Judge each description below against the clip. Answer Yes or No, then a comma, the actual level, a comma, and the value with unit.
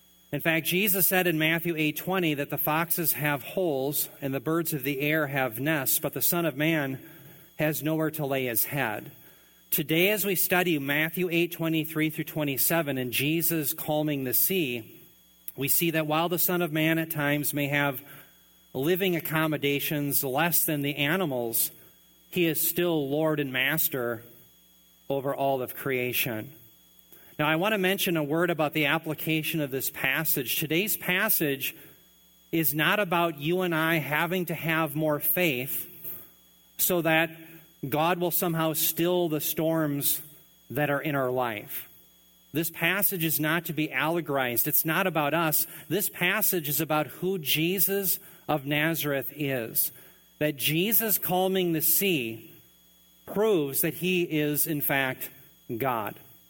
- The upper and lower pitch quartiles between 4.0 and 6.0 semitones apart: No, average, 3.3 semitones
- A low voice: No, medium, 155 Hz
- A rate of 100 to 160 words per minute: Yes, average, 150 wpm